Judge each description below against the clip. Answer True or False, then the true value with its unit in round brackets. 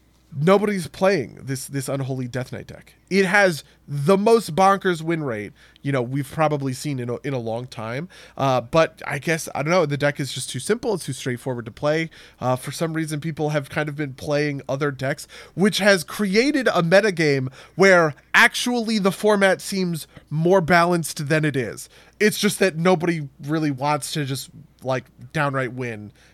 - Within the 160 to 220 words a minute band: True (185 wpm)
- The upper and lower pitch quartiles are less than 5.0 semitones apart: False (5.4 semitones)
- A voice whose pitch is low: False (150 Hz)